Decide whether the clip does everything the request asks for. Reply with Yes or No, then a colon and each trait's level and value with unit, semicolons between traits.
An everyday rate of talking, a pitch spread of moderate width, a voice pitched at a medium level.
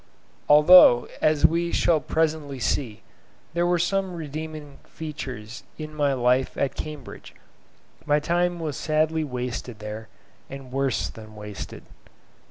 No: slow, 125 wpm; average, 4.0 semitones; medium, 150 Hz